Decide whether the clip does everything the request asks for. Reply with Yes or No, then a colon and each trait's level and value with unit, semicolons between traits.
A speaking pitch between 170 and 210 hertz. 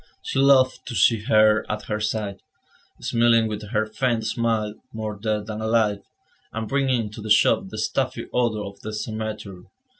No: low, 110 Hz